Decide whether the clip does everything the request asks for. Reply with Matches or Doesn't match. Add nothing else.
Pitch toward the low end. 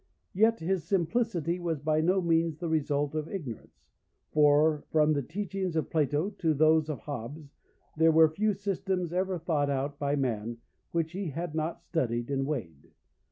Doesn't match